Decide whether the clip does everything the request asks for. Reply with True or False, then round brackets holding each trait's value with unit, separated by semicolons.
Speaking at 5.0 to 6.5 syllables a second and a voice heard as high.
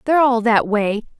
True (5.6 syllables/s; 235 Hz)